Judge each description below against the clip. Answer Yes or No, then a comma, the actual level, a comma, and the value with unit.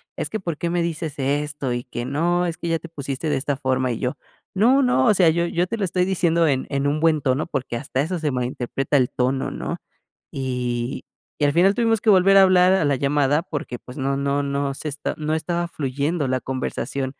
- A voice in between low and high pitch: Yes, medium, 145 Hz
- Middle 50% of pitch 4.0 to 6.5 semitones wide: Yes, average, 4.4 semitones